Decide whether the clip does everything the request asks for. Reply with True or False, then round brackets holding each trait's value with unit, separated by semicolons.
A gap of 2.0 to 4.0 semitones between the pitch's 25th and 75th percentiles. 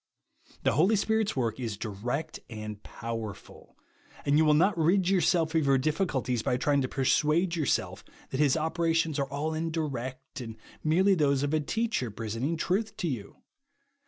False (4.8 semitones)